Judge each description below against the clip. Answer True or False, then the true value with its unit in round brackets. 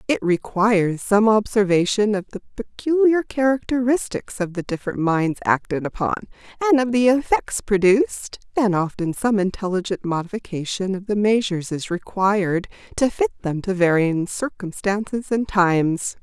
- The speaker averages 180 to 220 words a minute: False (135 wpm)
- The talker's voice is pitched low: False (205 Hz)